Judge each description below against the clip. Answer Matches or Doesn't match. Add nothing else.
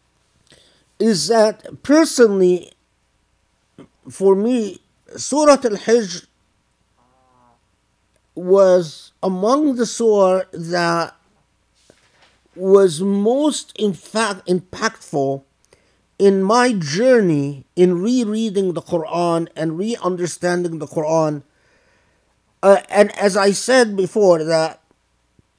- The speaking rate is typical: Doesn't match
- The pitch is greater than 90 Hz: Matches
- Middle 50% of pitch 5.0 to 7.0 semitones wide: Matches